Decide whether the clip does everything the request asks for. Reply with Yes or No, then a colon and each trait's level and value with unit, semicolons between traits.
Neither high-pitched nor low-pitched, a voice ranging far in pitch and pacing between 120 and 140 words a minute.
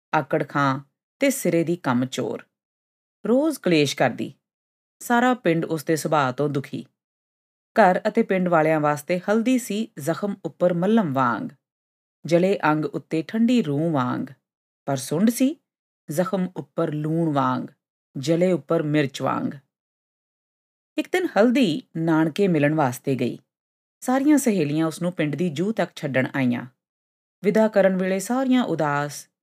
Yes: medium, 165 Hz; wide, 5.7 semitones; average, 135 wpm